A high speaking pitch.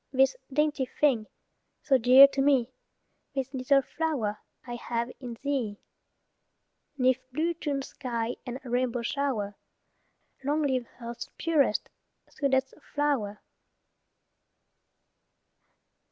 Yes: very high, 260 Hz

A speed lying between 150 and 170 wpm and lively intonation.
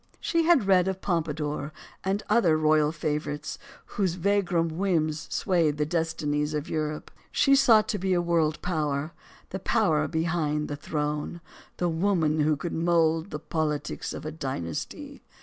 No: average, 155 wpm; average, 3.2 semitones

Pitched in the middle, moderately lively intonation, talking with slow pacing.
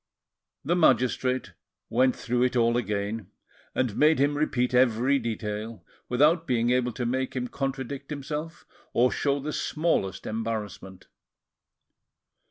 No: low, 125 Hz; average, 3.5 semitones; slow, 125 wpm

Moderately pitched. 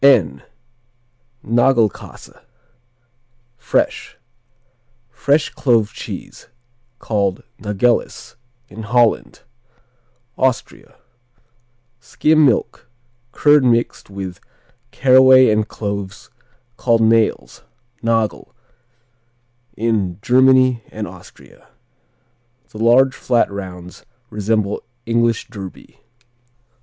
No: low, 115 Hz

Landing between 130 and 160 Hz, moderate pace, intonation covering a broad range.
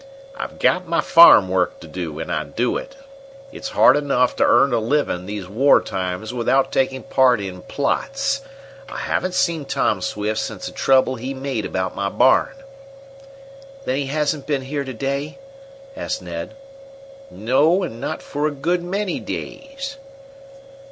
Yes: low, 135 Hz; average, 160 wpm; wide, 6.5 semitones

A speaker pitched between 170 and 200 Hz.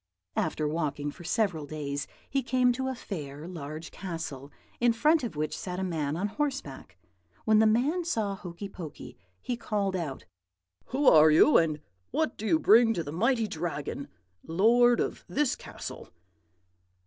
Yes: high, 190 Hz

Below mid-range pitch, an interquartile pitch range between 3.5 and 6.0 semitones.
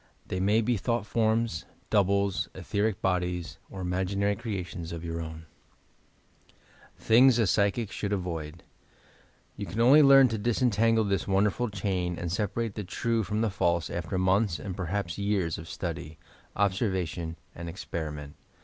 Yes: very low, 95 Hz; average, 3.9 semitones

